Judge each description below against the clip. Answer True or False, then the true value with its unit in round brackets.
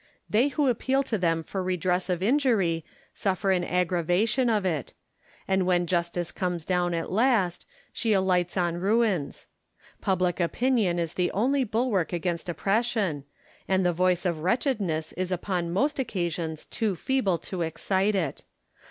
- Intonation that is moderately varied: True (3.9 semitones)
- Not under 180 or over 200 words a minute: False (150 wpm)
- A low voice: False (185 Hz)